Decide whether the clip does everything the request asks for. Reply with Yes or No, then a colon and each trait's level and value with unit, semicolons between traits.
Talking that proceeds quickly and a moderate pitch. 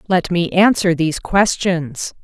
No: slow, 135 wpm; medium, 175 Hz